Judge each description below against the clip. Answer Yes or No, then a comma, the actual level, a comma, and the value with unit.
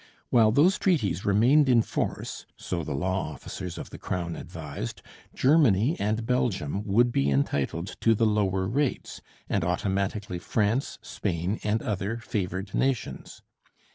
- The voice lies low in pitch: Yes, low, 100 Hz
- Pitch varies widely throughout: No, average, 4.5 semitones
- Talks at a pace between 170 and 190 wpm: No, average, 140 wpm